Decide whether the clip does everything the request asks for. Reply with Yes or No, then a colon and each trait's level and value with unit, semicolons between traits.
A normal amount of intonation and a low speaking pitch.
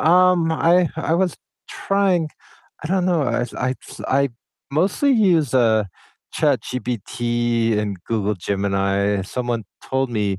No: wide, 8.0 semitones; low, 130 Hz